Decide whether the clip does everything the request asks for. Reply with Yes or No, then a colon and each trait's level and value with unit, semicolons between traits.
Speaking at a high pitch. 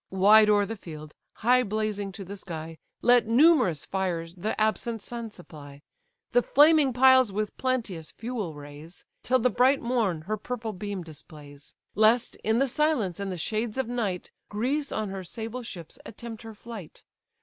Yes: high, 215 Hz